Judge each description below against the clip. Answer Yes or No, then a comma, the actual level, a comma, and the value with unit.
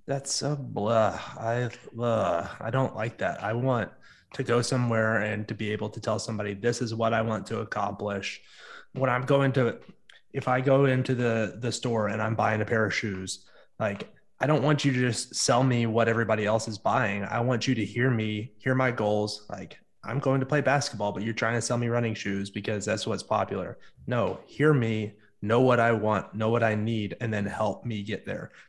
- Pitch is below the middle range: Yes, low, 115 Hz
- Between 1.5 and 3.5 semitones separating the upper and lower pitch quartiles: Yes, average, 2.9 semitones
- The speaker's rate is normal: No, fast, 220 wpm